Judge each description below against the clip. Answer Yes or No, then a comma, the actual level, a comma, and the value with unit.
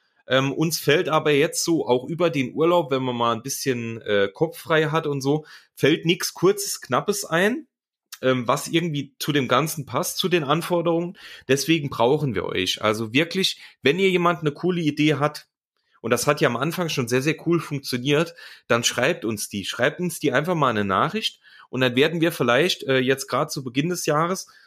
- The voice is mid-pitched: Yes, medium, 150 Hz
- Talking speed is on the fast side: Yes, fast, 200 wpm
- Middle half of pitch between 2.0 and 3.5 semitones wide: No, average, 4.5 semitones